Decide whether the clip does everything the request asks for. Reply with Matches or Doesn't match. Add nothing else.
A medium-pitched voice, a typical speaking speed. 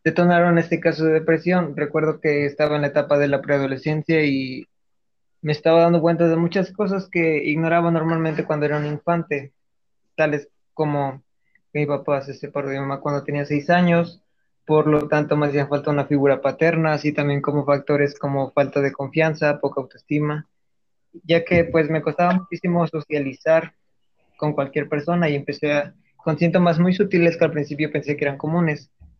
Matches